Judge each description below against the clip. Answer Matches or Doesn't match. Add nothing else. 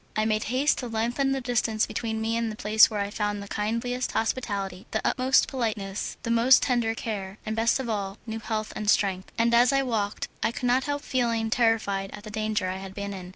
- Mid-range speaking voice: Doesn't match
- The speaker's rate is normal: Doesn't match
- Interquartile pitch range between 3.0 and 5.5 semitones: Doesn't match